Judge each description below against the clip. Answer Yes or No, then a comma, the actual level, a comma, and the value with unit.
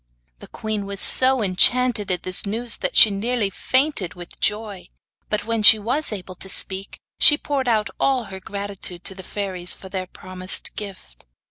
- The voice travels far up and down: No, average, 3.5 semitones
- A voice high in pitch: Yes, high, 200 Hz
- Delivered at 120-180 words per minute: Yes, average, 175 wpm